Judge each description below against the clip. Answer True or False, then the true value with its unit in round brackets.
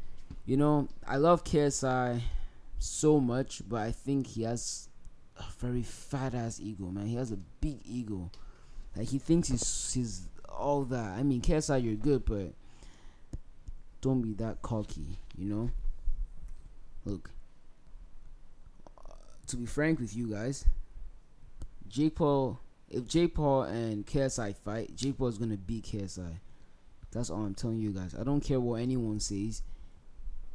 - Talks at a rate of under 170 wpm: True (140 wpm)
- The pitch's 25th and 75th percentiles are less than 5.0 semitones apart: False (5.5 semitones)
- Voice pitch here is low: True (115 Hz)